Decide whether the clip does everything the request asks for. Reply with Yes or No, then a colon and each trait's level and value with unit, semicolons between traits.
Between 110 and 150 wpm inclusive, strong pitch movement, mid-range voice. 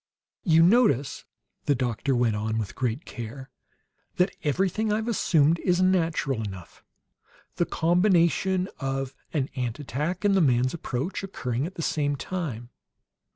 Yes: average, 140 wpm; wide, 6.3 semitones; medium, 145 Hz